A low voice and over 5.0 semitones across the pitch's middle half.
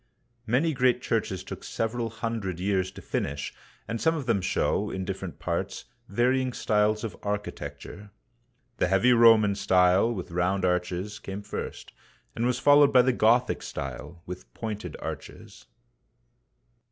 No: low, 105 Hz; average, 4.3 semitones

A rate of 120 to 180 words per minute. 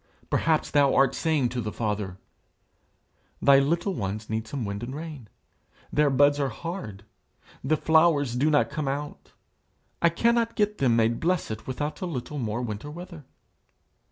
Yes: average, 155 wpm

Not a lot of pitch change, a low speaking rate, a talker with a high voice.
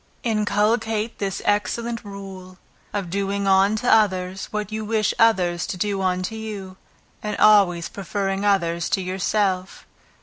Yes: narrow, 2.2 semitones; slow, 130 wpm; high, 200 Hz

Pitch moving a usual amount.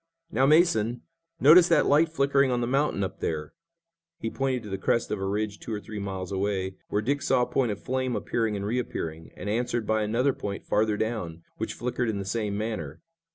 Yes: average, 4.1 semitones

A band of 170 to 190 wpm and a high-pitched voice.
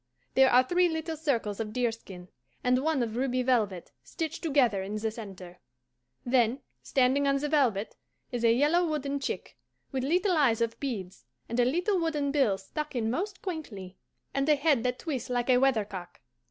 Yes: average, 180 wpm; very high, 255 Hz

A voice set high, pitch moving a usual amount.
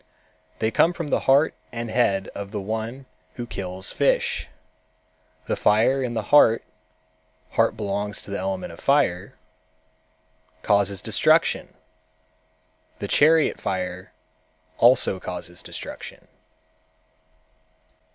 No: low, 105 Hz; average, 4.5 semitones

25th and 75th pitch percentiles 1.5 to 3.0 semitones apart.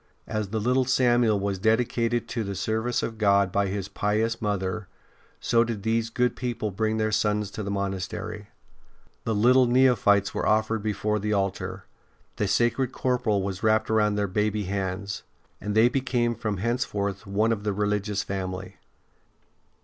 Yes: narrow, 2.4 semitones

